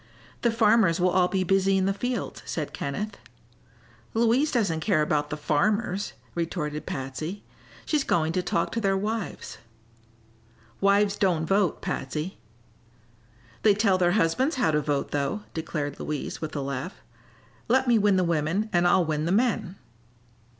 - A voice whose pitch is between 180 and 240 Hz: Yes, medium, 185 Hz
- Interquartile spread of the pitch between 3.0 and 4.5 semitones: No, average, 5.0 semitones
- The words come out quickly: No, average, 155 wpm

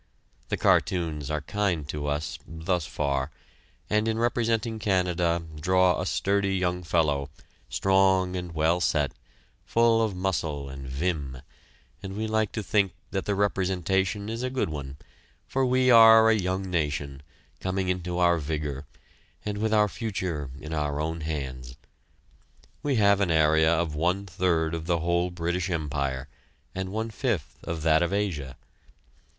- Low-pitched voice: Yes, very low, 90 Hz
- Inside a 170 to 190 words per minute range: No, average, 155 wpm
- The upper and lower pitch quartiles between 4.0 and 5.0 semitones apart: Yes, average, 4.6 semitones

